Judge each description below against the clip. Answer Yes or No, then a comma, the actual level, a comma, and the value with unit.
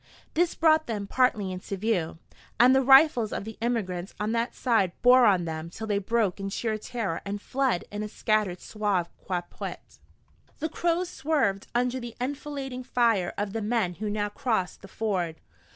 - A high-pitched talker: Yes, high, 220 Hz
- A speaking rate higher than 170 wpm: Yes, average, 180 wpm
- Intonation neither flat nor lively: Yes, average, 4.2 semitones